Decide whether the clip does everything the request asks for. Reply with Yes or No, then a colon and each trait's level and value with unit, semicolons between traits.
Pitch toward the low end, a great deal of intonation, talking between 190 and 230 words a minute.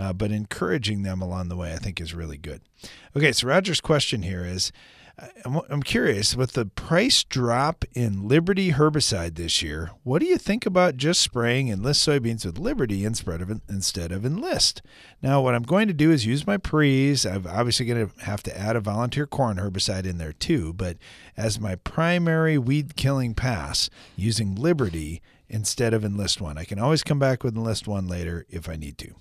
Yes: low, 115 Hz; wide, 7.2 semitones; average, 195 wpm